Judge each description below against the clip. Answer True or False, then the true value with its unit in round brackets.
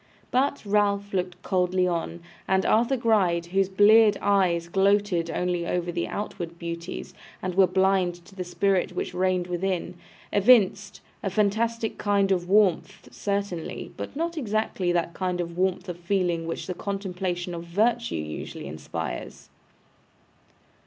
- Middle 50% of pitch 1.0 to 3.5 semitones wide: True (2.5 semitones)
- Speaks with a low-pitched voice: False (185 Hz)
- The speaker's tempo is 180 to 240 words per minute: False (140 wpm)